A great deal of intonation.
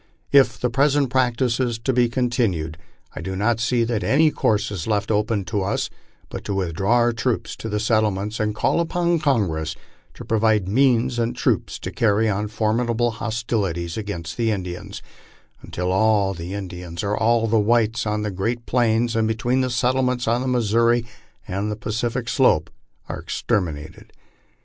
No: average, 3.0 semitones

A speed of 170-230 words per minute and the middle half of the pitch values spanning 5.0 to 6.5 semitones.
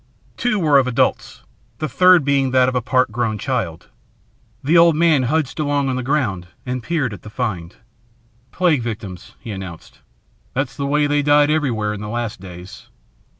Yes: average, 180 wpm; wide, 5.4 semitones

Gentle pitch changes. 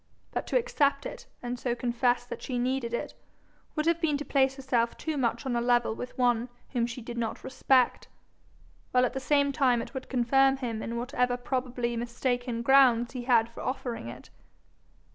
Yes: narrow, 2.1 semitones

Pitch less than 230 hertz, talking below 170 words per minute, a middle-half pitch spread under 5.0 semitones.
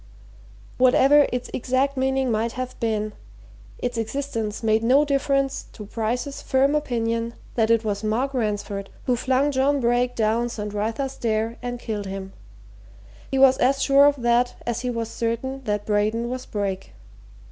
No: high, 240 Hz; average, 160 wpm; average, 3.3 semitones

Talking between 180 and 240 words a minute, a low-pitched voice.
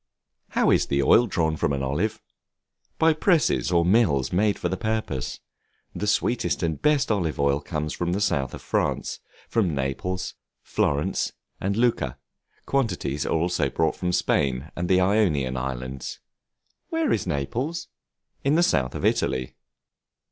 No: average, 150 wpm; very low, 85 Hz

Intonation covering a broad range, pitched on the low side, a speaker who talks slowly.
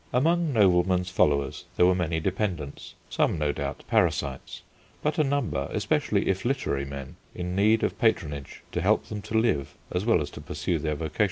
No: wide, 7.2 semitones; very low, 90 Hz; average, 180 wpm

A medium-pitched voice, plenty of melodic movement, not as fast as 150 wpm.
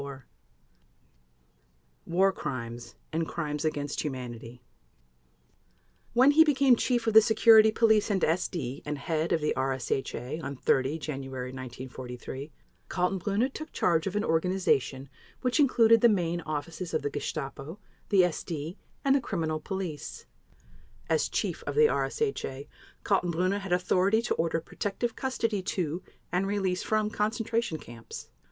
Yes: medium, 175 Hz; wide, 6.9 semitones; slow, 135 wpm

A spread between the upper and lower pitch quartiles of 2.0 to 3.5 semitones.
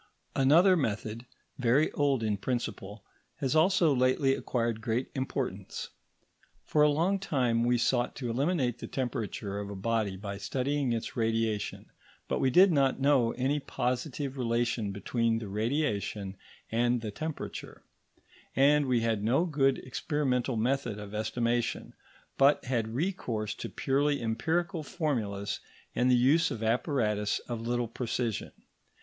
No: average, 3.9 semitones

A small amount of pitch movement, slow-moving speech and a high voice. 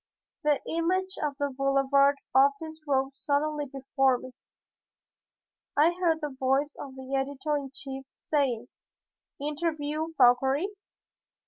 Yes: narrow, 2.2 semitones; slow, 115 wpm; very high, 280 Hz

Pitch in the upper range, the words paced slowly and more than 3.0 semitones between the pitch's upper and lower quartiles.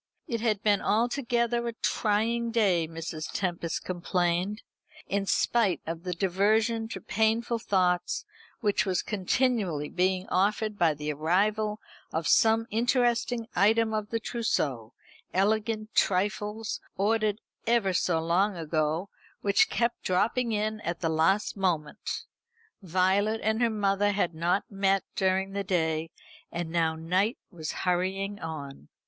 Yes: high, 195 Hz; slow, 130 wpm; average, 4.0 semitones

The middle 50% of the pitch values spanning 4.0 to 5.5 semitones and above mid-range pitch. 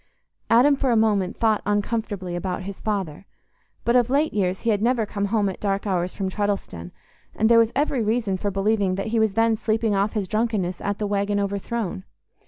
No: narrow, 2.6 semitones; high, 205 Hz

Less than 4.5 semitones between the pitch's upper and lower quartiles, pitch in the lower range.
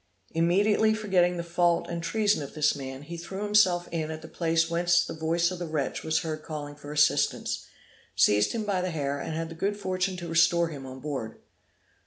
No: average, 2.9 semitones; medium, 170 Hz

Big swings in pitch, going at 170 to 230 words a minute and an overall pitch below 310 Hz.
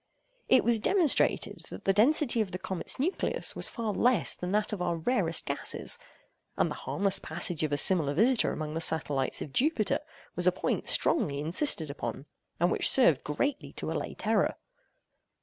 Yes: wide, 7.5 semitones; average, 175 wpm; medium, 185 Hz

